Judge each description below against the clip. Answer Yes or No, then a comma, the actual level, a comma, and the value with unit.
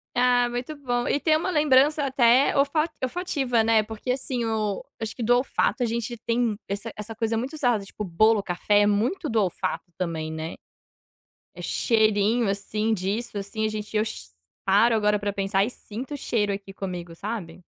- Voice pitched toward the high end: Yes, high, 220 Hz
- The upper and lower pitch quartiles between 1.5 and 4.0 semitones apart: Yes, average, 3.3 semitones